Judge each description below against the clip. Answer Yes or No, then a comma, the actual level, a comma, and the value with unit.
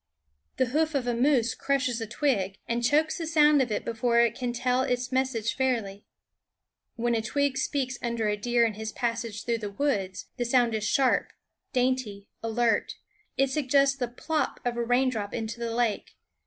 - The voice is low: No, high, 240 Hz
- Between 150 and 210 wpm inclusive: Yes, average, 180 wpm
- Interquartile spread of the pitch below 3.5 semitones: Yes, narrow, 2.6 semitones